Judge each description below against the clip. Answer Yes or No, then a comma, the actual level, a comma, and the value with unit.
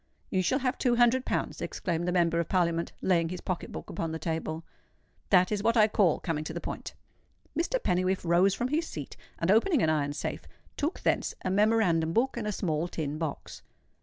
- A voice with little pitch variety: No, average, 5.3 semitones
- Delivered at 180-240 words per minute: Yes, fast, 205 wpm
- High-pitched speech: No, medium, 180 Hz